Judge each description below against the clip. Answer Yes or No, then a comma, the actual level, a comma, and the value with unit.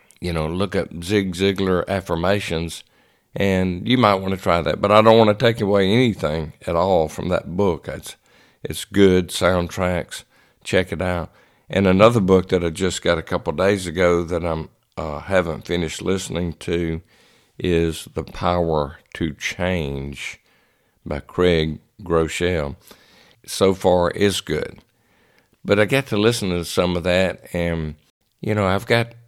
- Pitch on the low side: Yes, very low, 90 Hz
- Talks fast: No, average, 160 wpm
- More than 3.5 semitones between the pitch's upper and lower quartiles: No, average, 2.8 semitones